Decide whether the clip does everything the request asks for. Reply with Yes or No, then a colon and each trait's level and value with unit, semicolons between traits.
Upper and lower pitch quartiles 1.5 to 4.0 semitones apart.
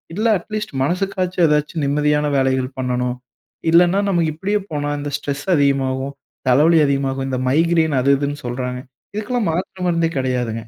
No: average, 4.6 semitones